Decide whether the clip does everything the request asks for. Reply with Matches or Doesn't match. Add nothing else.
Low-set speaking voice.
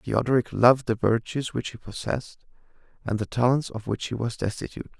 Matches